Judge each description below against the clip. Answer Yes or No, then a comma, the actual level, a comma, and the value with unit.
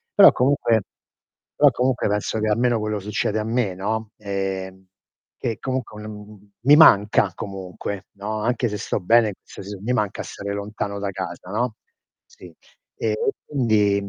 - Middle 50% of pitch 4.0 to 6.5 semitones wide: No, narrow, 2.5 semitones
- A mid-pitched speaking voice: No, low, 105 Hz